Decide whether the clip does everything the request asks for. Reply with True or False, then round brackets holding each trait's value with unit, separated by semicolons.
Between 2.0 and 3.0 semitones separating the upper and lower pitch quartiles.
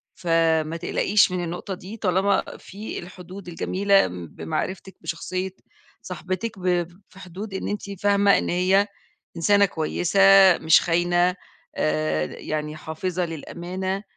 True (2.7 semitones)